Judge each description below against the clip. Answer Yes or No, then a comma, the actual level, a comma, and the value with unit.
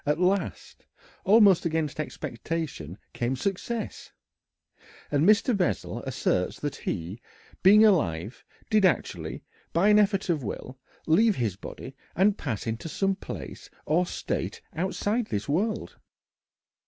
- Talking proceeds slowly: Yes, slow, 125 wpm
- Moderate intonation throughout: No, wide, 7.7 semitones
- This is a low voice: No, medium, 165 Hz